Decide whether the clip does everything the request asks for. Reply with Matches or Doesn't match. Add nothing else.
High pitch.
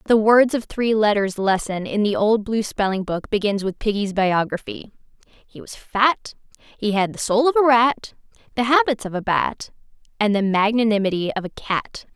Matches